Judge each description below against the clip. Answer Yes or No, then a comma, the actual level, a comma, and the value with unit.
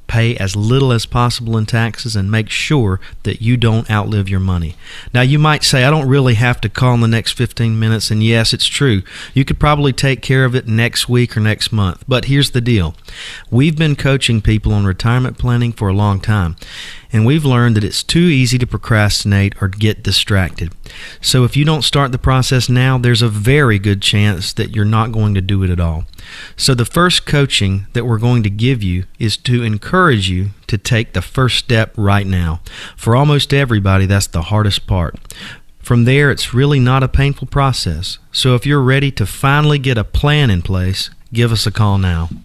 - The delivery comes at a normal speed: No, fast, 210 wpm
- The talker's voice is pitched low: Yes, low, 115 Hz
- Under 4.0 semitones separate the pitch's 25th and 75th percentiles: No, average, 4.4 semitones